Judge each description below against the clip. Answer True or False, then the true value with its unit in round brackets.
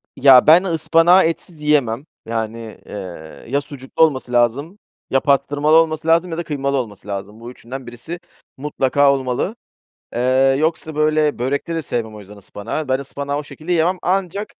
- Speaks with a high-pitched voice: False (140 Hz)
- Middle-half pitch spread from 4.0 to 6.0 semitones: True (4.7 semitones)